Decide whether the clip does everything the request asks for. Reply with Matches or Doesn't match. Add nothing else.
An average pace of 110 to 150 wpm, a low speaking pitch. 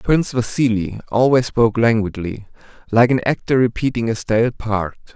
Matches